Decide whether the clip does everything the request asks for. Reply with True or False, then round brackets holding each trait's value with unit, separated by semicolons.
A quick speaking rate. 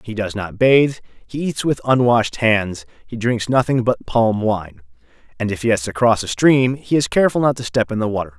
True (230 wpm)